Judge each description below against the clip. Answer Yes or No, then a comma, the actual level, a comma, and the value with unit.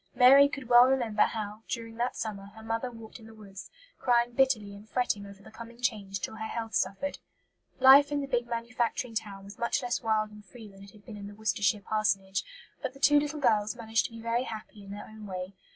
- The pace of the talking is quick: Yes, fast, 230 wpm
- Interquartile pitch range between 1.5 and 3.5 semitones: Yes, average, 3.1 semitones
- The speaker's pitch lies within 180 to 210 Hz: No, high, 225 Hz